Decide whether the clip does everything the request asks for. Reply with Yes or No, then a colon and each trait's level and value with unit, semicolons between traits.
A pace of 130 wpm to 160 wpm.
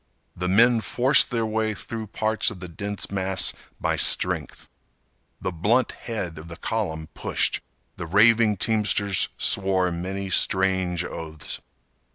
Yes: slow, 135 wpm